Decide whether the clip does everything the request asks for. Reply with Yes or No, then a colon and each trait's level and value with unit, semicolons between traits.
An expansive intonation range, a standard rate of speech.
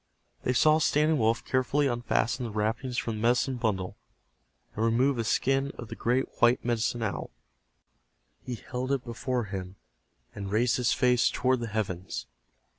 No: average, 2.7 semitones; average, 160 wpm